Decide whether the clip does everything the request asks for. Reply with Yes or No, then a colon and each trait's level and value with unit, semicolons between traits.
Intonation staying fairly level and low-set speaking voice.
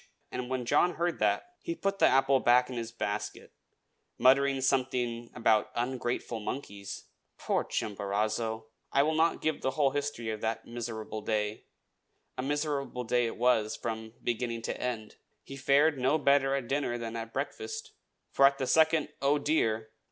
No: average, 3.7 semitones; low, 125 Hz